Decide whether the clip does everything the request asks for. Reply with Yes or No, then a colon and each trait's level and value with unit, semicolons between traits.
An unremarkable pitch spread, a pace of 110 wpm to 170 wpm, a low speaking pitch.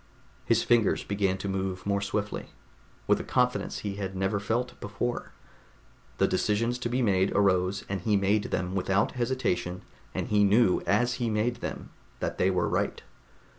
Yes: average, 3.6 semitones; average, 165 wpm; low, 100 Hz